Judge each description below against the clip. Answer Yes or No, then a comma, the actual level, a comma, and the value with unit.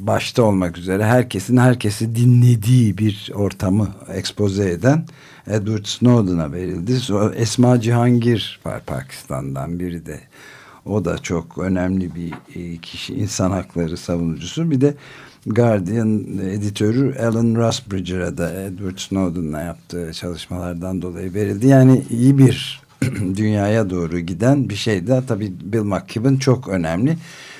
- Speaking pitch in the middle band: No, low, 105 Hz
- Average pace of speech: Yes, average, 115 wpm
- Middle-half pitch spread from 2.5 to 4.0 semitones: No, average, 4.9 semitones